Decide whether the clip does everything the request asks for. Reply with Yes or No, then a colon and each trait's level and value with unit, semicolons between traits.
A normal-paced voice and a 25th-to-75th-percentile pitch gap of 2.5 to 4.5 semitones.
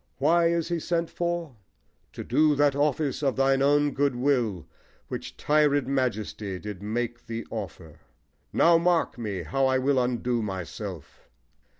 No: average, 150 wpm; average, 5.1 semitones